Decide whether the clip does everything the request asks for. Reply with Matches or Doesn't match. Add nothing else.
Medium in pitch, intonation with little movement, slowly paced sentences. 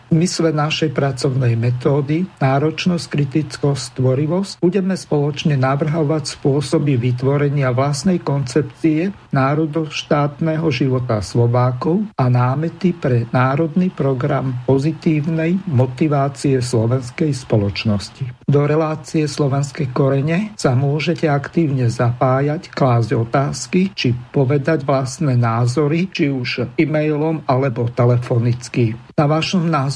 Doesn't match